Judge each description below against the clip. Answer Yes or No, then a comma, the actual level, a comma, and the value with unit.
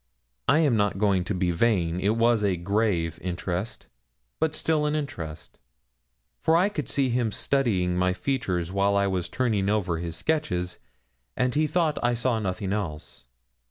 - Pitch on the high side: No, low, 105 Hz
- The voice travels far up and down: Yes, wide, 6.0 semitones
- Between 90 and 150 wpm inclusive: No, average, 165 wpm